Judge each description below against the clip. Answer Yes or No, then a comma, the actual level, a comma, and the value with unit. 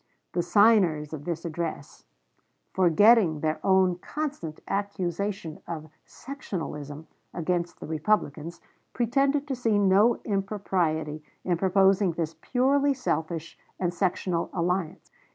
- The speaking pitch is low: No, medium, 180 Hz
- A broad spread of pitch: No, average, 4.3 semitones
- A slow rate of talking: Yes, slow, 110 wpm